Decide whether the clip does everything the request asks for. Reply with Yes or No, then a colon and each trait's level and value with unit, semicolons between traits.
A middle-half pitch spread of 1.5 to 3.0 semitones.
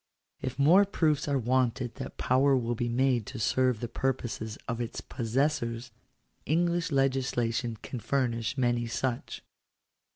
Yes: narrow, 2.5 semitones